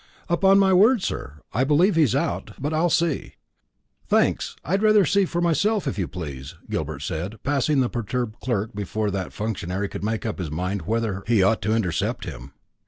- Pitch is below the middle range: Yes, low, 115 Hz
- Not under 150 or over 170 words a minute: No, average, 180 wpm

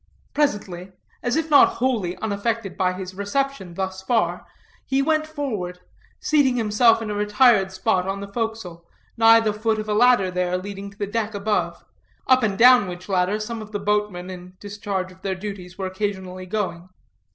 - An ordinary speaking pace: Yes, average, 180 wpm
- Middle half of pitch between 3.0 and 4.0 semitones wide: Yes, average, 3.3 semitones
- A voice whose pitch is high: Yes, high, 205 Hz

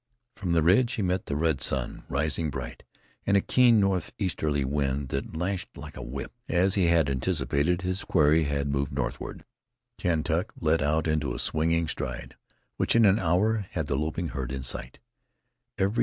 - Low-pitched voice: Yes, very low, 80 Hz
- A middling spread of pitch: Yes, average, 4.5 semitones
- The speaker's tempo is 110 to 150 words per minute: No, average, 170 wpm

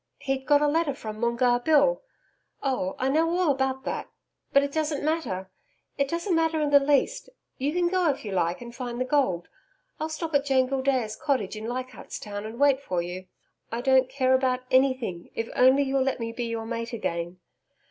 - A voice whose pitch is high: Yes, very high, 260 Hz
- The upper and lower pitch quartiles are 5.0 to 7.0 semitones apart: No, average, 3.7 semitones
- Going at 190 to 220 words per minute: Yes, average, 200 wpm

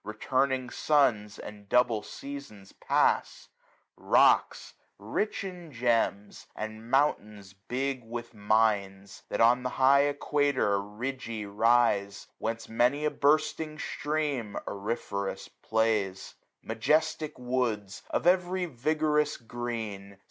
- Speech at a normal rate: No, slow, 105 wpm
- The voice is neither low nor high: No, low, 120 Hz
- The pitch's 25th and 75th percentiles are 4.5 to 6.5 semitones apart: Yes, average, 5.1 semitones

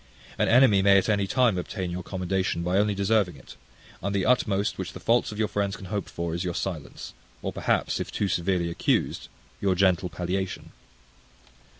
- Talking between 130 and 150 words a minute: No, average, 190 wpm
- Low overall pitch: Yes, very low, 95 Hz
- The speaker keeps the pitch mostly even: Yes, narrow, 2.3 semitones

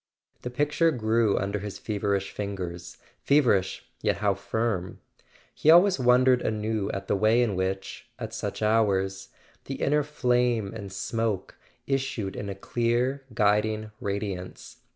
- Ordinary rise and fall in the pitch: Yes, average, 3.9 semitones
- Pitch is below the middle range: Yes, low, 110 Hz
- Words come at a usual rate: No, slow, 130 wpm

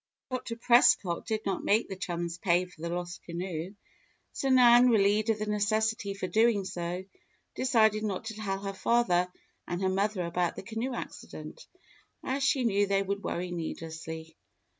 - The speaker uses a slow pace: No, average, 160 wpm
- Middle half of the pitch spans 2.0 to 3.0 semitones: No, average, 4.0 semitones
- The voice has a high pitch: Yes, high, 200 Hz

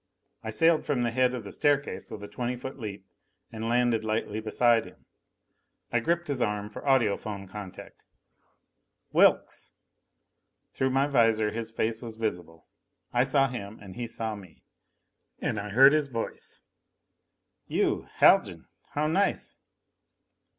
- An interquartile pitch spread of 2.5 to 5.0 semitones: Yes, average, 3.8 semitones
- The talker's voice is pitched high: No, low, 115 Hz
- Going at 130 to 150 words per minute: Yes, average, 145 wpm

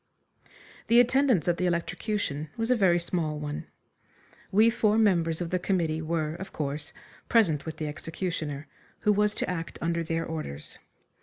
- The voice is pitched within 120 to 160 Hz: No, medium, 170 Hz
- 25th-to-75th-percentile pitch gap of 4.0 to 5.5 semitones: Yes, average, 4.6 semitones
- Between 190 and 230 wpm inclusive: No, average, 160 wpm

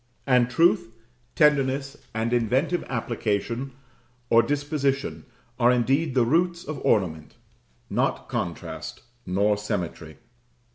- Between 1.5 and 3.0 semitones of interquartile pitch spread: No, average, 4.2 semitones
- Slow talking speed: Yes, slow, 100 wpm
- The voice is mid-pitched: No, low, 125 Hz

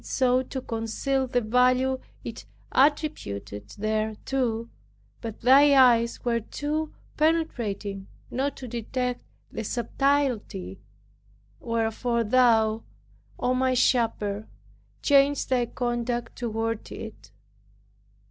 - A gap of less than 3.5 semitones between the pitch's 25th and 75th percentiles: Yes, average, 2.8 semitones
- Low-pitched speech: No, high, 240 Hz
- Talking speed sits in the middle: No, slow, 100 wpm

